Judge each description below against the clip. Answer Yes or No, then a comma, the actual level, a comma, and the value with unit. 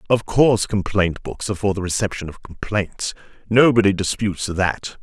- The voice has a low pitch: Yes, low, 100 Hz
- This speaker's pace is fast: No, average, 145 wpm